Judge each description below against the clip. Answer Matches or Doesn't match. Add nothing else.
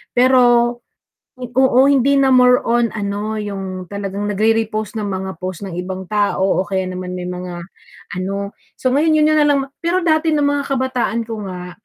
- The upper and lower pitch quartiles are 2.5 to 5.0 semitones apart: Doesn't match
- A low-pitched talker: Doesn't match